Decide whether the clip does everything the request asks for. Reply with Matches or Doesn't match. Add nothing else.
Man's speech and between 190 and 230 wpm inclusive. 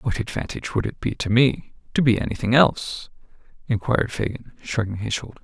Doesn't match